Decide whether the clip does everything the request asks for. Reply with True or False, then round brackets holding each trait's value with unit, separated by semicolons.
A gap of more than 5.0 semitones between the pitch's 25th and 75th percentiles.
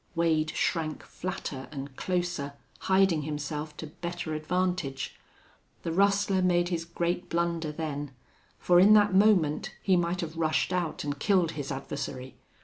False (3.1 semitones)